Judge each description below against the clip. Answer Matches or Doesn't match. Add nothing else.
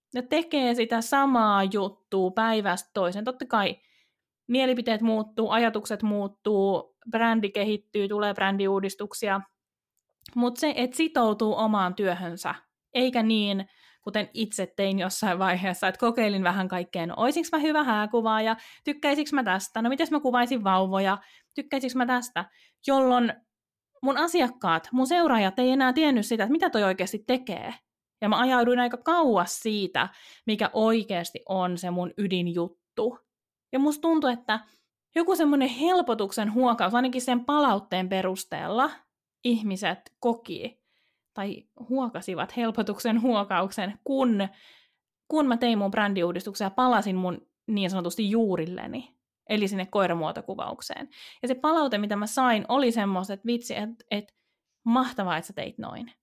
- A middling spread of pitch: Matches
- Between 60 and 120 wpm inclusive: Doesn't match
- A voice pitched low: Doesn't match